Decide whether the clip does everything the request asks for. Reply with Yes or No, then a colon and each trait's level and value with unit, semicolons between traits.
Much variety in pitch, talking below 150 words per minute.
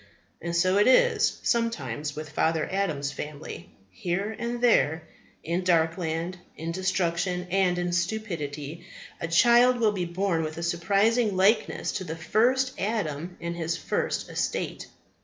No: average, 4.2 semitones; average, 140 wpm